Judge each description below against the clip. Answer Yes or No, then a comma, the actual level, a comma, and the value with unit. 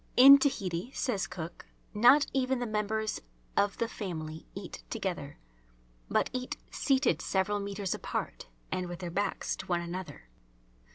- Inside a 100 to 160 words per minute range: Yes, average, 145 wpm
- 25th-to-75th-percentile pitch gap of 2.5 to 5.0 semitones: No, wide, 5.5 semitones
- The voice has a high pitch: Yes, high, 205 Hz